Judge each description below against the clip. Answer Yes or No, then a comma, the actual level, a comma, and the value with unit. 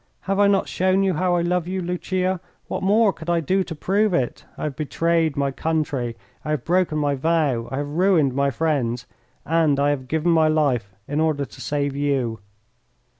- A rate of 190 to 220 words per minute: Yes, average, 200 wpm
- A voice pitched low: No, medium, 155 Hz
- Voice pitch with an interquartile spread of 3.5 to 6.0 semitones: Yes, average, 4.2 semitones